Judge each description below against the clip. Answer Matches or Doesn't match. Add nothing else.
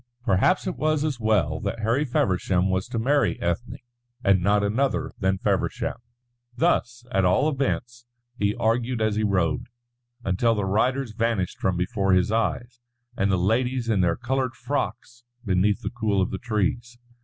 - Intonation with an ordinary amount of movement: Matches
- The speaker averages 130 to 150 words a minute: Doesn't match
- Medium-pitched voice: Doesn't match